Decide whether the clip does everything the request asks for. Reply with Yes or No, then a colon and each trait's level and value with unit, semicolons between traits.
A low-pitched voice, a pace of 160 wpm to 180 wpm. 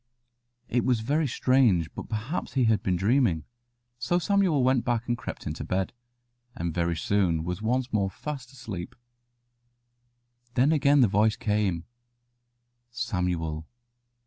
No: low, 110 Hz; slow, 135 wpm